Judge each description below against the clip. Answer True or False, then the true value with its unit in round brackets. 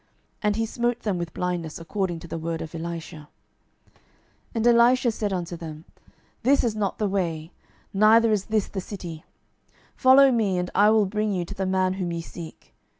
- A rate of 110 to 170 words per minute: False (190 wpm)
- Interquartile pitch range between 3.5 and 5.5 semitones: True (4.3 semitones)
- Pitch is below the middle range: False (190 Hz)